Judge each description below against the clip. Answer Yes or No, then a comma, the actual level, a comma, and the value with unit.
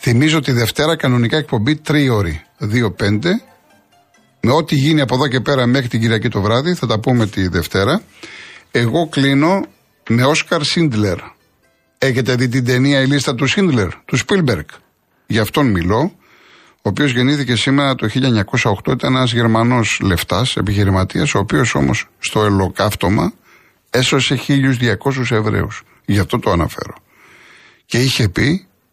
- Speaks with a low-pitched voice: Yes, low, 125 Hz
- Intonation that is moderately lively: Yes, average, 4.8 semitones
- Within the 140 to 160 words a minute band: Yes, average, 145 wpm